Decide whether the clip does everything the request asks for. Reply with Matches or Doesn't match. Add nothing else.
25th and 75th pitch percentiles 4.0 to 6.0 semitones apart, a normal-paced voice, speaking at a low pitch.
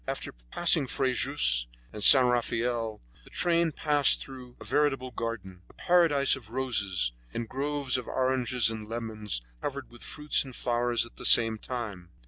Doesn't match